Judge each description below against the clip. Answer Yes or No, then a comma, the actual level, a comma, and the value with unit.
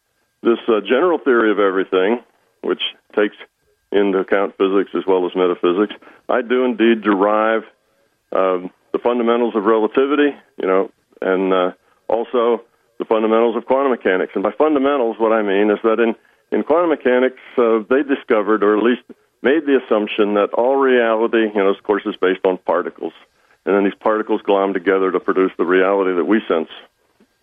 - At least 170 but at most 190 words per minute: Yes, average, 175 wpm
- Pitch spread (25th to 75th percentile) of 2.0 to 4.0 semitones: Yes, average, 3.3 semitones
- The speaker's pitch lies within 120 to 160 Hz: No, low, 110 Hz